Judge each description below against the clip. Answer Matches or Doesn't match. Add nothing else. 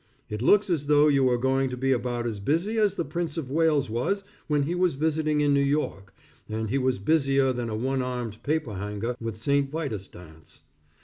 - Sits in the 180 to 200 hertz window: Doesn't match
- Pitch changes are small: Doesn't match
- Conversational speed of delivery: Doesn't match